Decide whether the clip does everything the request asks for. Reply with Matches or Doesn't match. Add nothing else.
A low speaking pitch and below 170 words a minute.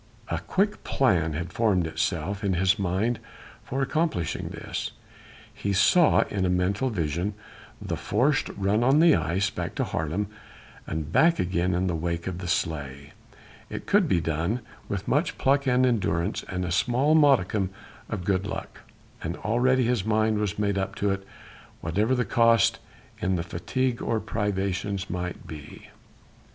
Matches